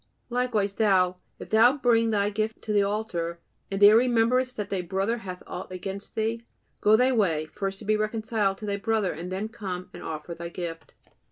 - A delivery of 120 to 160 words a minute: No, average, 190 wpm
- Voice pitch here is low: No, high, 205 Hz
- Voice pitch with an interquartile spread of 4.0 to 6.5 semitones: No, average, 3.2 semitones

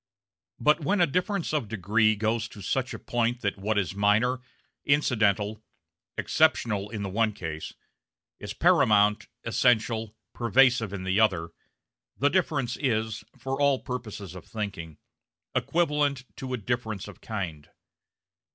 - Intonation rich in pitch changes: No, average, 4.1 semitones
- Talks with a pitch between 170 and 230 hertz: No, low, 110 Hz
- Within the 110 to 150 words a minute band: Yes, average, 140 wpm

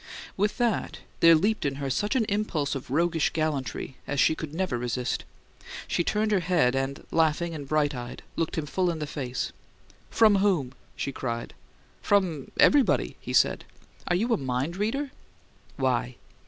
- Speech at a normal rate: Yes, average, 170 wpm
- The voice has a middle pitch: Yes, medium, 155 Hz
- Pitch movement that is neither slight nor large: No, wide, 6.5 semitones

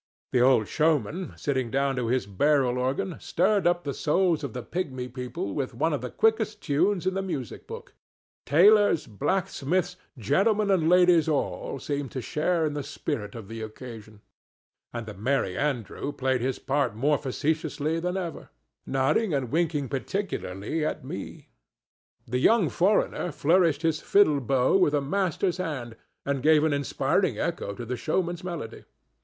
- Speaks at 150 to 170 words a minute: Yes, average, 160 wpm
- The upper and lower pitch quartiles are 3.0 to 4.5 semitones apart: No, wide, 5.5 semitones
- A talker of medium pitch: Yes, medium, 145 Hz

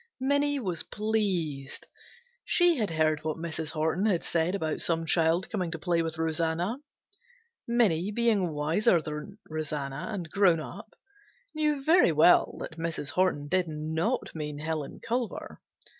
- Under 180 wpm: Yes, average, 145 wpm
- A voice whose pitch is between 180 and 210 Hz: No, medium, 165 Hz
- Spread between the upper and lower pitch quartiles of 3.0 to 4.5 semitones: No, average, 4.9 semitones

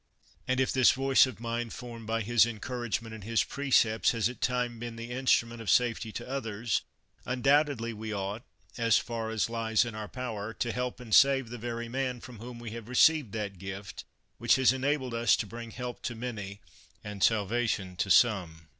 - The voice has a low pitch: Yes, low, 115 Hz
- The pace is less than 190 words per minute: No, average, 200 wpm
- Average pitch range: No, narrow, 2.3 semitones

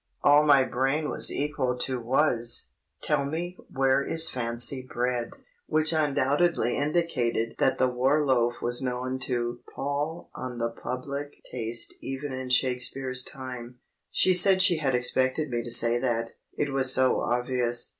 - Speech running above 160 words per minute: No, average, 150 wpm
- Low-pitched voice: Yes, low, 130 Hz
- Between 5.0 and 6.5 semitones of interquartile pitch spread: No, average, 2.8 semitones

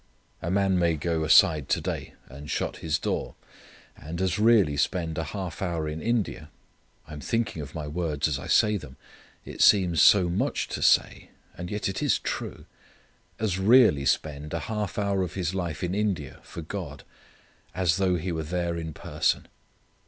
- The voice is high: No, very low, 85 Hz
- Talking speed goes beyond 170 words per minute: Yes, average, 180 wpm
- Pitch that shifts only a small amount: No, average, 3.8 semitones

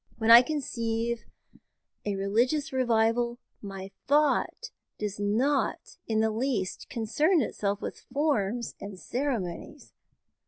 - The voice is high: Yes, high, 230 Hz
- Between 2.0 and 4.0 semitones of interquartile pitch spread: No, average, 4.7 semitones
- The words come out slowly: Yes, slow, 110 wpm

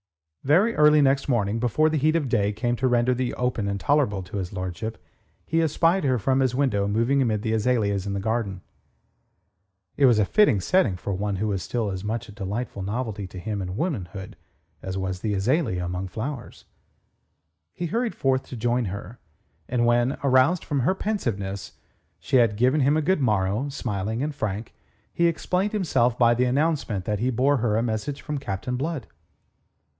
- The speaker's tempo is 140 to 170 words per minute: No, average, 190 wpm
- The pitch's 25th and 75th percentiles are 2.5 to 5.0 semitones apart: No, wide, 5.5 semitones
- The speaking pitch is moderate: No, low, 120 Hz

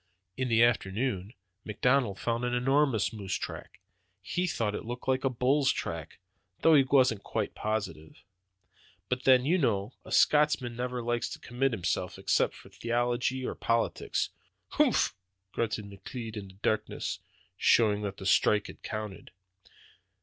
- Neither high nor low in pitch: No, low, 115 Hz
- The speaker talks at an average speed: Yes, average, 150 wpm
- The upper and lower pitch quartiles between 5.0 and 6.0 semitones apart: No, average, 3.7 semitones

